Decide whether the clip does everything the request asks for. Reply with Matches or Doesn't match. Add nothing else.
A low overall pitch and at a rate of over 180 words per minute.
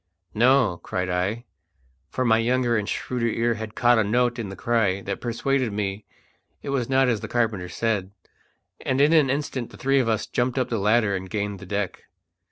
Matches